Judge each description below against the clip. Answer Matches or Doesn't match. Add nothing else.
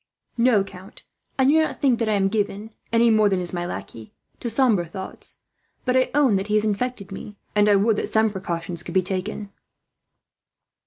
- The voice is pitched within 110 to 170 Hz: Doesn't match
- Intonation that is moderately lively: Matches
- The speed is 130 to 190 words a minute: Doesn't match